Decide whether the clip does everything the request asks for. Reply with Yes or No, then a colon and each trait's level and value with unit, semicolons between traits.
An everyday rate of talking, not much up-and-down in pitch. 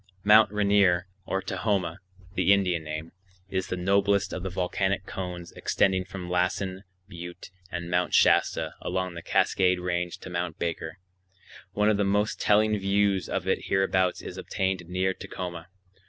Yes: average, 155 wpm; narrow, 2.0 semitones